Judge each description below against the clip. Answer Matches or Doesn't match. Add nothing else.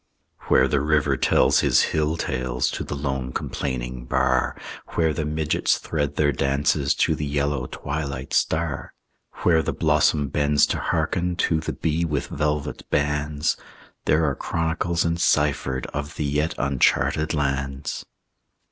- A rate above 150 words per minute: Doesn't match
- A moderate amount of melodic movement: Doesn't match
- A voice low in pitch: Matches